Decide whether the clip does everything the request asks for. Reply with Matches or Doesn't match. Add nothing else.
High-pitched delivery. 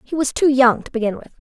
Matches